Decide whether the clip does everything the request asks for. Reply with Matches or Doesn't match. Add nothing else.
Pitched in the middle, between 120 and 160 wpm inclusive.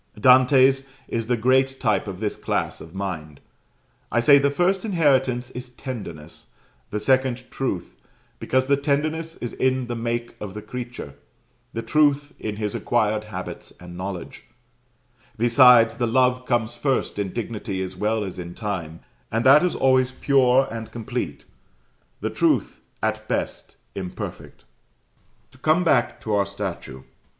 Doesn't match